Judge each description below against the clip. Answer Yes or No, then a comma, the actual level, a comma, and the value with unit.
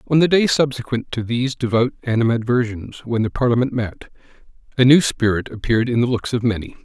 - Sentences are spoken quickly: No, average, 185 wpm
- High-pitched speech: No, low, 120 Hz